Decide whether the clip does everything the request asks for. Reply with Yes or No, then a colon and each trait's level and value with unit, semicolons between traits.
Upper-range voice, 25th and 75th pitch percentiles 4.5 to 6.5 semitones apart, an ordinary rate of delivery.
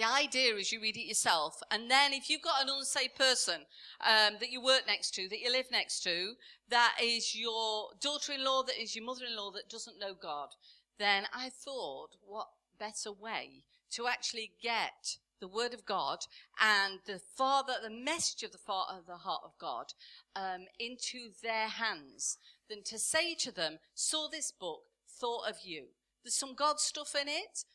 No: high, 235 Hz; average, 4.0 semitones; average, 180 wpm